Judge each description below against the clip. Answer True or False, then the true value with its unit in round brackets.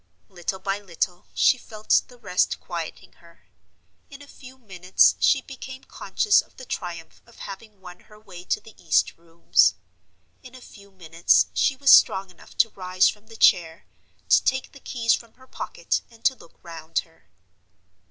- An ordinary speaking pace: True (175 wpm)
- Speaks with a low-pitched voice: False (200 Hz)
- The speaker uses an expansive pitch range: True (6.0 semitones)